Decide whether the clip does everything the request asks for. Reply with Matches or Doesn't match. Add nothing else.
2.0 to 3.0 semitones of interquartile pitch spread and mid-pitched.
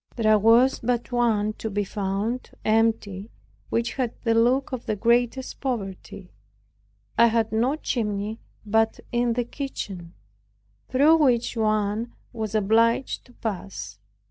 Doesn't match